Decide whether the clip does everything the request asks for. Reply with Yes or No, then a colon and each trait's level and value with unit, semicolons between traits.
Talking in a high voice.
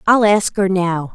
Yes: high, 195 Hz